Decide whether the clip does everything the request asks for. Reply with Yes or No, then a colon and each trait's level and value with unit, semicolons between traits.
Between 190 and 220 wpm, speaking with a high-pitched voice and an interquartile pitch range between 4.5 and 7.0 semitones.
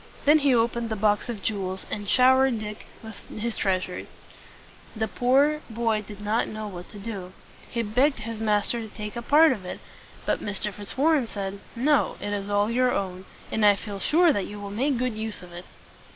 No: average, 195 wpm; high, 215 Hz; average, 3.4 semitones